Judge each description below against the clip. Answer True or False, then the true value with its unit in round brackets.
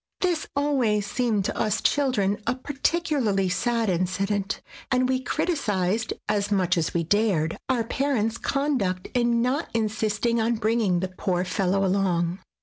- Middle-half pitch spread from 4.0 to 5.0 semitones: True (4.7 semitones)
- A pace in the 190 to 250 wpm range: False (145 wpm)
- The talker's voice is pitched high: True (215 Hz)